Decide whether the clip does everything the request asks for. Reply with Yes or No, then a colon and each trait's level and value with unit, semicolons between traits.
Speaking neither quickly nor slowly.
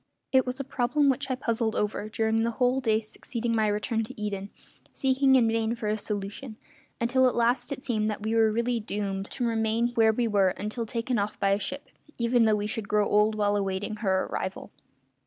No: fast, 210 wpm